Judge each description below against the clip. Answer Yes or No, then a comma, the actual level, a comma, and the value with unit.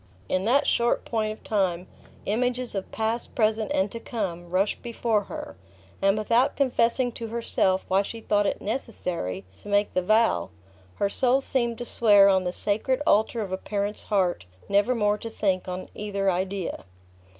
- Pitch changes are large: No, average, 3.3 semitones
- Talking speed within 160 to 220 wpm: Yes, average, 170 wpm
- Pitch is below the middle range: No, high, 210 Hz